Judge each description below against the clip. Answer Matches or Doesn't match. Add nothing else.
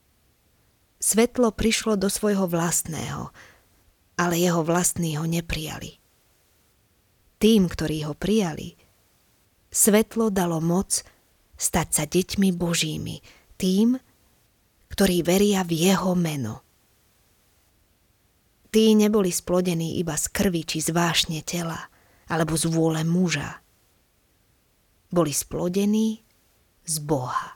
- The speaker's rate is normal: Doesn't match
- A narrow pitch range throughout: Doesn't match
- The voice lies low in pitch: Doesn't match